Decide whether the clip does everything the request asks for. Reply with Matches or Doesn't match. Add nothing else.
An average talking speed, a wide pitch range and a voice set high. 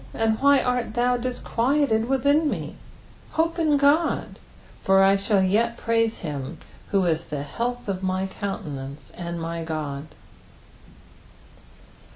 Doesn't match